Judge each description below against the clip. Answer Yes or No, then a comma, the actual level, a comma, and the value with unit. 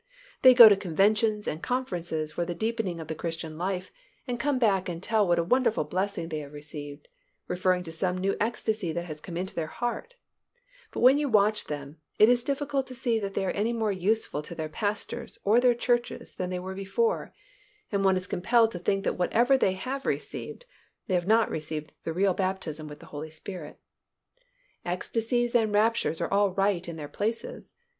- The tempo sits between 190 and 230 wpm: Yes, average, 200 wpm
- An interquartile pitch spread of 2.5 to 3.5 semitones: No, average, 5.0 semitones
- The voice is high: Yes, high, 195 Hz